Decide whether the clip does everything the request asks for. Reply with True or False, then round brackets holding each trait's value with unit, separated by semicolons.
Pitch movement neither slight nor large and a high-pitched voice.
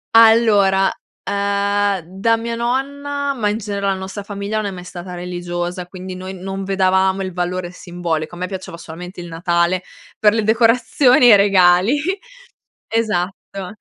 True (3.2 semitones; 195 Hz)